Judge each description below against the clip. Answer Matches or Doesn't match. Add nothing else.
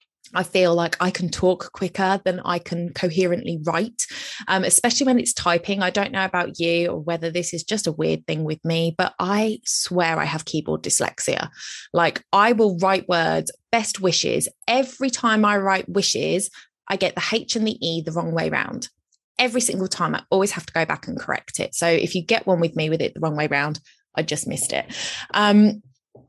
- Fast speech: Matches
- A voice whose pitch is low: Doesn't match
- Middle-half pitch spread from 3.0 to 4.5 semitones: Matches